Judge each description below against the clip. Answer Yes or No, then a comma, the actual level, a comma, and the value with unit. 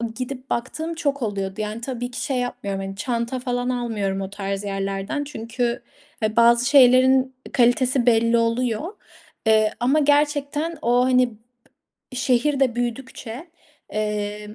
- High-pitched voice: Yes, high, 245 Hz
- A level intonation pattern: No, average, 3.3 semitones